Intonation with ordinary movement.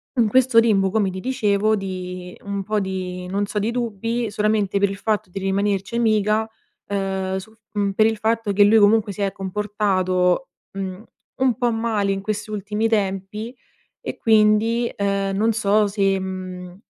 No: narrow, 2.2 semitones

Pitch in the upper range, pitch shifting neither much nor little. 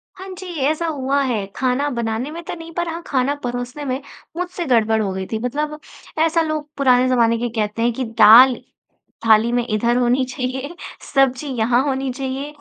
Yes: very high, 255 Hz; average, 3.7 semitones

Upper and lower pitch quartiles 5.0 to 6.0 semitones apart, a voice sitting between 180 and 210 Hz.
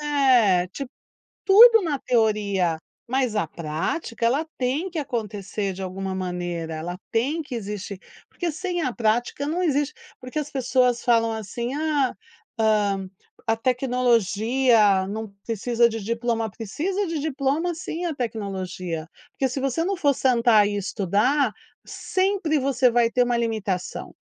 No: wide, 5.6 semitones; high, 235 Hz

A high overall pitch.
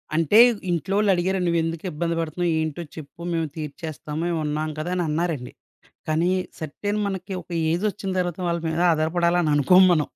No: medium, 170 Hz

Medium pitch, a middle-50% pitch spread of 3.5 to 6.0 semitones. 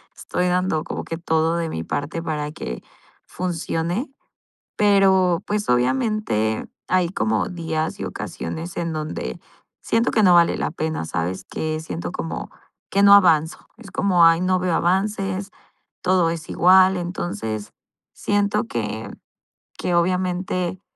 No: medium, 170 Hz; average, 3.1 semitones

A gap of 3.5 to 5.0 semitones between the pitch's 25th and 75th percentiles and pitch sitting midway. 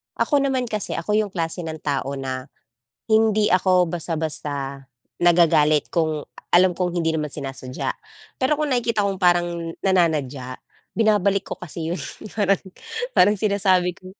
Yes: average, 4.5 semitones; medium, 175 Hz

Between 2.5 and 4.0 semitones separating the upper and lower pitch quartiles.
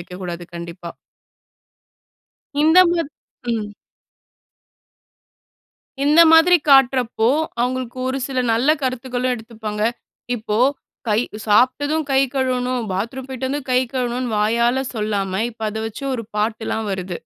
Yes: average, 3.7 semitones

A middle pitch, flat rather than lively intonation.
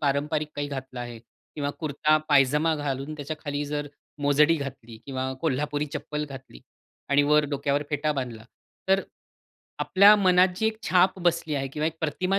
Yes: medium, 145 Hz; narrow, 2.0 semitones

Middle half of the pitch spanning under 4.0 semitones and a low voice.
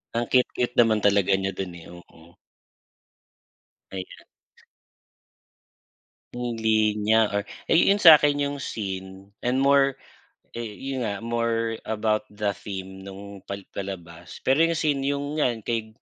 No: average, 4.4 semitones; low, 110 Hz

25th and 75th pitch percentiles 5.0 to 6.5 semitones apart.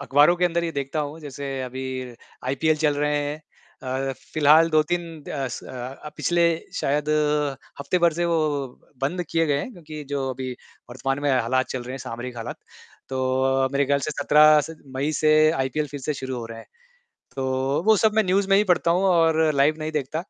No: average, 3.5 semitones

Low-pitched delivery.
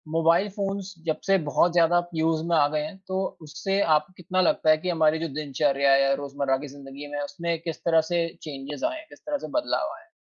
No: medium, 160 Hz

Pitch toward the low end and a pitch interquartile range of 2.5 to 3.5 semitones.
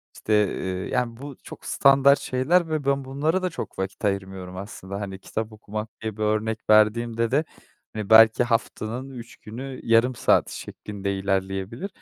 No: low, 110 Hz; average, 4.5 semitones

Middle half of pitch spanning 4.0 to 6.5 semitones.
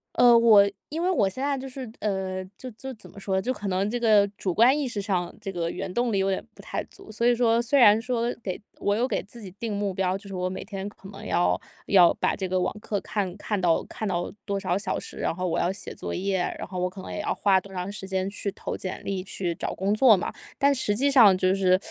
No: average, 3.6 semitones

